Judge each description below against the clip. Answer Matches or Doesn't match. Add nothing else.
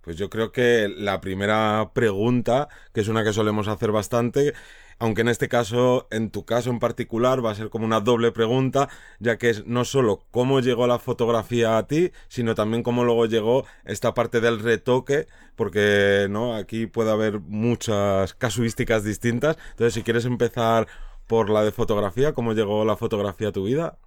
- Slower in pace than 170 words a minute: Doesn't match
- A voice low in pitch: Matches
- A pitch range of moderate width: Doesn't match